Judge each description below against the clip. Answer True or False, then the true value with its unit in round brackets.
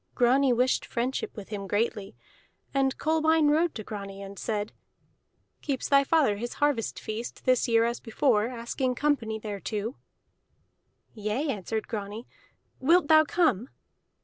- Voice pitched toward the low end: False (235 Hz)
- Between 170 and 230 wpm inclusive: False (135 wpm)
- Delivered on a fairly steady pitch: False (4.7 semitones)